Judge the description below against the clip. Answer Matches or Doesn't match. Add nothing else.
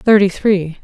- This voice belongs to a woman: Matches